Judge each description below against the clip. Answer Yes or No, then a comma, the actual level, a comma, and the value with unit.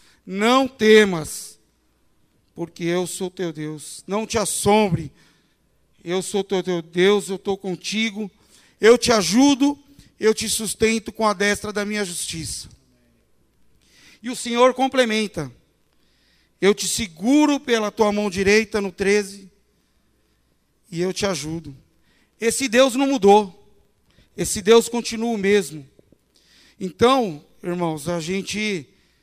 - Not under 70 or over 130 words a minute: Yes, slow, 120 wpm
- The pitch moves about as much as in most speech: Yes, average, 3.9 semitones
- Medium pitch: No, high, 205 Hz